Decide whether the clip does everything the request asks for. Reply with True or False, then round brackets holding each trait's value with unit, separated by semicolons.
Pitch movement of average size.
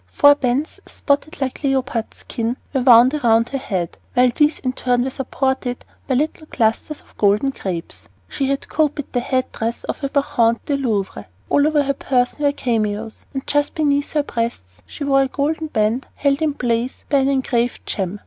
True (3.5 semitones)